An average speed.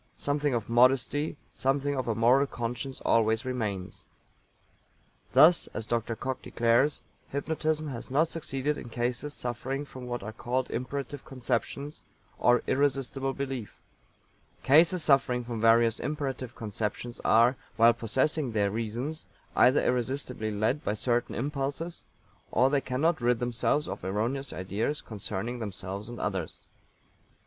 No: slow, 130 wpm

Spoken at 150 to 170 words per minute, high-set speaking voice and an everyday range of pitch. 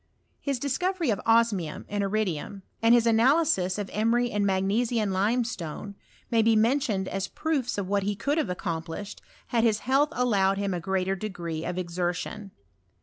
Yes: average, 165 wpm; high, 205 Hz; average, 3.8 semitones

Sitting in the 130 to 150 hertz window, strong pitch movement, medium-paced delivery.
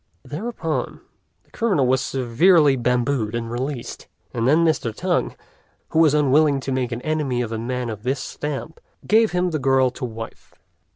No: low, 135 Hz; average, 4.3 semitones; average, 170 wpm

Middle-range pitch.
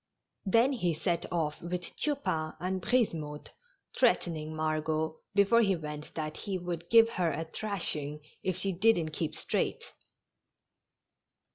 Yes: medium, 170 Hz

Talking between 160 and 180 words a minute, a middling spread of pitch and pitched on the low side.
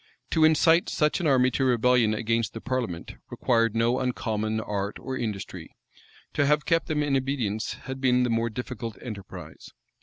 Yes: average, 170 wpm; average, 3.4 semitones; low, 125 Hz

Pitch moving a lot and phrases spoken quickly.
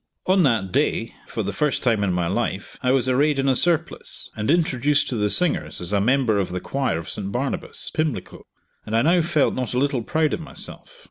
Yes: wide, 6.0 semitones; fast, 220 wpm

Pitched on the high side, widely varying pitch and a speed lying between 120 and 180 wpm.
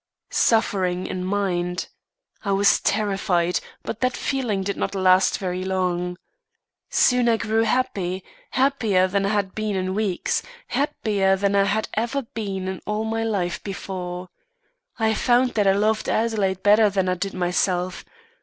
No: high, 200 Hz; average, 2.9 semitones; average, 155 wpm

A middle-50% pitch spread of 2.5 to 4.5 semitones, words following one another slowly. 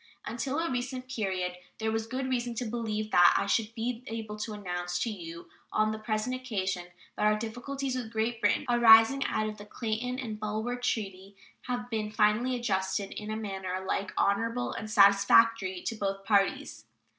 No: average, 3.2 semitones; average, 180 wpm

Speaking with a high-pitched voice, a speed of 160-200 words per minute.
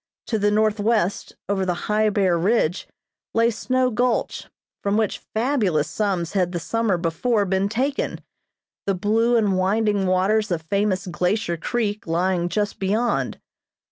No: high, 205 Hz; average, 140 wpm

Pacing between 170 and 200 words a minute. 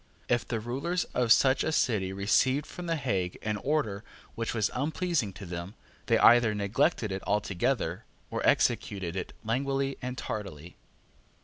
No: average, 150 wpm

